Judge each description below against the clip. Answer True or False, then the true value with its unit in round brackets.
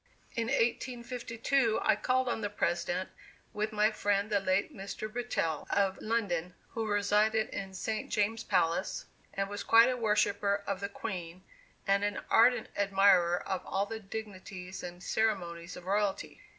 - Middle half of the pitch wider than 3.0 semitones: False (2.7 semitones)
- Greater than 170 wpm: False (150 wpm)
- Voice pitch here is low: False (205 Hz)